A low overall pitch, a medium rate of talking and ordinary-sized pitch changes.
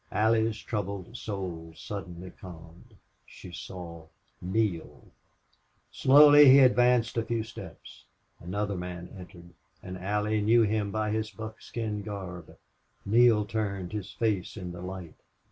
No: low, 100 Hz; slow, 125 wpm; average, 3.6 semitones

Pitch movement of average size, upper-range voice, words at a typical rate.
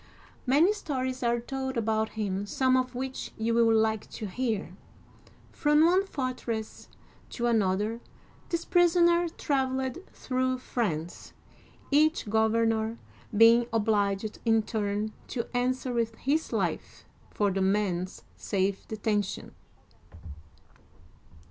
No: average, 3.5 semitones; high, 230 Hz; slow, 110 wpm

